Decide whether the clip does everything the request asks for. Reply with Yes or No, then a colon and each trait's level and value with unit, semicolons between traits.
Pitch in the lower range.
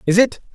No: high, 215 Hz